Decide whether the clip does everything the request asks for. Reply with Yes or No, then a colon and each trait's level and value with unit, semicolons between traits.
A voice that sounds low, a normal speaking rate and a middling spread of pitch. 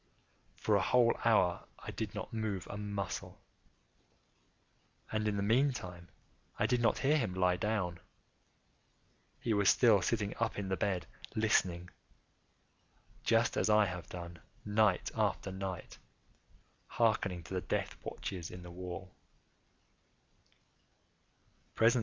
No: low, 100 Hz; slow, 125 wpm; average, 3.4 semitones